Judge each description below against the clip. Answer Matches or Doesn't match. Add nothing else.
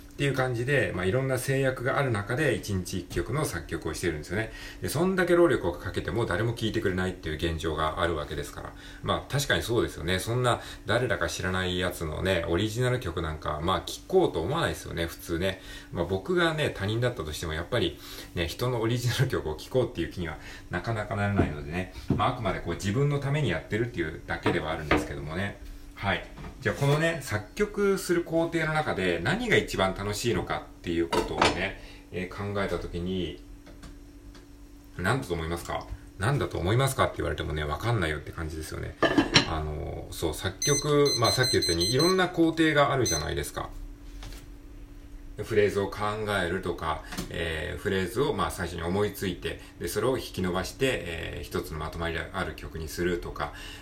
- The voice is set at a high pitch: Doesn't match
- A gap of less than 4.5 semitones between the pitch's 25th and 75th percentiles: Doesn't match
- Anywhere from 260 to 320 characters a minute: Doesn't match